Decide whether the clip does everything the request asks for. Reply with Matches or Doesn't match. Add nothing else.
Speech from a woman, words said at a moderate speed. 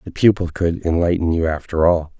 Doesn't match